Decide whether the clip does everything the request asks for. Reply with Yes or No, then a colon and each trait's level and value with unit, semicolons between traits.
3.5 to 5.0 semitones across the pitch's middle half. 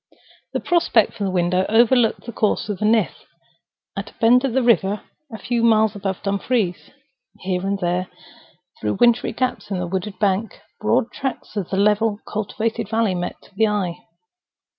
No: average, 3.1 semitones